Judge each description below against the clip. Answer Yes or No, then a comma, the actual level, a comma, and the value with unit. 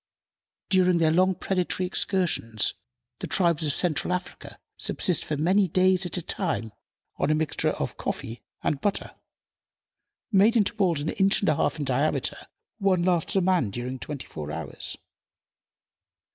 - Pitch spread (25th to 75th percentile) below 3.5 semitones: No, average, 4.6 semitones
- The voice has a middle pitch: Yes, medium, 175 Hz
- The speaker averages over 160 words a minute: No, average, 155 wpm